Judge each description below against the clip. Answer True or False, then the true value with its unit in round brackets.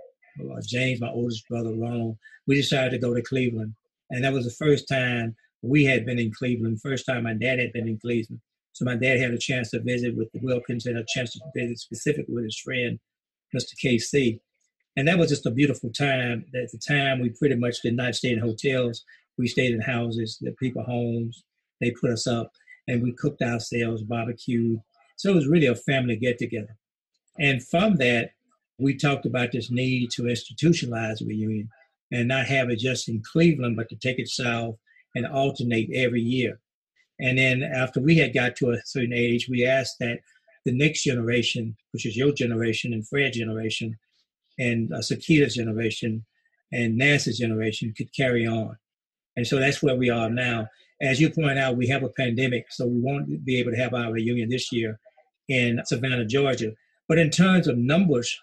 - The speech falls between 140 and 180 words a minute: False (195 wpm)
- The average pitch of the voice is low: True (125 Hz)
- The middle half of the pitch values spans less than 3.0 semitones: True (2.5 semitones)